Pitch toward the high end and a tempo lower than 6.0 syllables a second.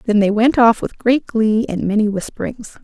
Yes: high, 220 Hz; 5.0 syllables/s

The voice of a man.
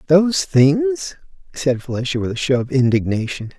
Yes: male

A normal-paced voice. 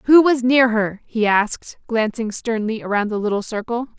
Yes: average, 180 wpm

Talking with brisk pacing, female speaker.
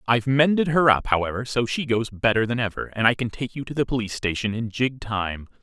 No: fast, 245 wpm; male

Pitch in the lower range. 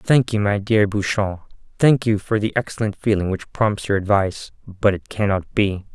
Yes: low, 105 Hz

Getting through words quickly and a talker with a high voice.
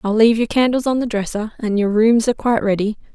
Yes: fast, 250 wpm; high, 225 Hz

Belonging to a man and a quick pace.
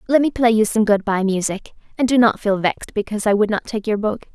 No: female; fast, 275 wpm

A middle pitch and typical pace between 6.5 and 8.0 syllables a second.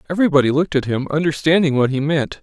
Yes: medium, 150 Hz; 7.3 syllables/s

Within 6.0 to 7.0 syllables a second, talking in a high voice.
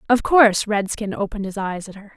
Yes: 6.2 syllables/s; high, 210 Hz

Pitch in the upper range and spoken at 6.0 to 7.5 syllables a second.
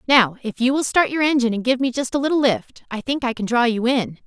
Yes: very high, 250 Hz; 6.2 syllables/s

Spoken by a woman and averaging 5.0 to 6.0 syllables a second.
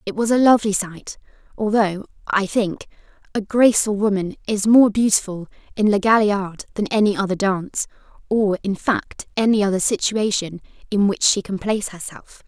Yes: female; 5.1 syllables/s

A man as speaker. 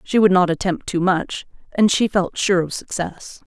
No: female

